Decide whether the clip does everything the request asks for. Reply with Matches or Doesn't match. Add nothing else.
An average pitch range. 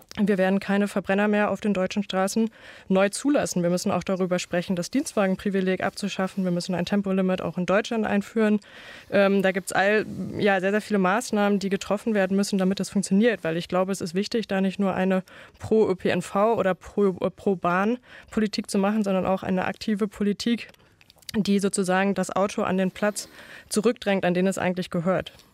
Doesn't match